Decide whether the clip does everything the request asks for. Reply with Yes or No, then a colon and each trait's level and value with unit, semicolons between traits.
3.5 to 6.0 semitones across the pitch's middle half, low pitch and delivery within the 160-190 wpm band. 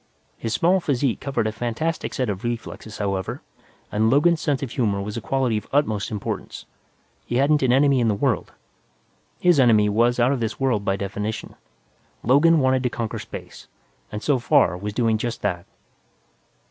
Yes: average, 4.3 semitones; low, 120 Hz; average, 175 wpm